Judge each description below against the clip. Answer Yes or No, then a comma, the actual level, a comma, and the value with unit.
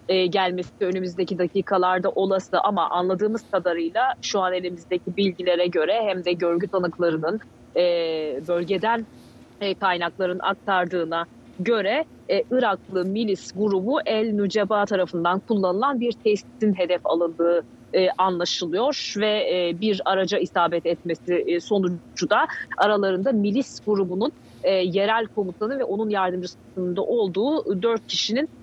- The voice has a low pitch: No, high, 190 Hz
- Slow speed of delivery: No, average, 120 wpm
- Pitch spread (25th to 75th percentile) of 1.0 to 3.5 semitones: Yes, average, 2.9 semitones